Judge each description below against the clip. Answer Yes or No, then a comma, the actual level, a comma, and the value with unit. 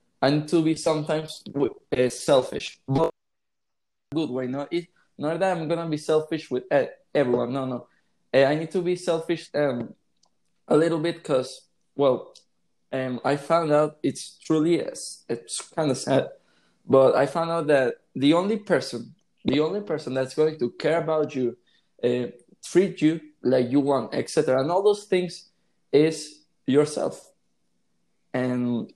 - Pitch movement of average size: Yes, average, 4.3 semitones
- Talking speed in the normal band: Yes, average, 145 wpm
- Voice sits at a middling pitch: Yes, medium, 150 Hz